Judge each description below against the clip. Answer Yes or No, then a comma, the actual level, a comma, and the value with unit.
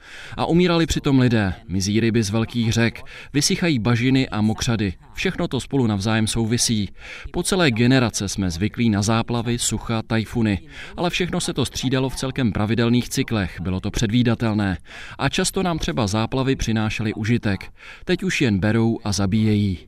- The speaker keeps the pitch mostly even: No, average, 3.8 semitones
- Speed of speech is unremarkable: Yes, average, 155 wpm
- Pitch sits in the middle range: No, low, 115 Hz